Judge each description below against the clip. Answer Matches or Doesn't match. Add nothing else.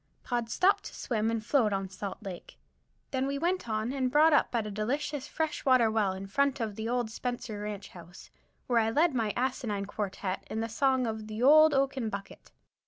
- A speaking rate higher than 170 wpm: Matches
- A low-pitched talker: Doesn't match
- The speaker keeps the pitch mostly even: Doesn't match